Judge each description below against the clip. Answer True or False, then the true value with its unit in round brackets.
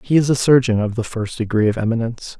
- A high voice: False (120 Hz)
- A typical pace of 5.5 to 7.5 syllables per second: True (6.6 syllables/s)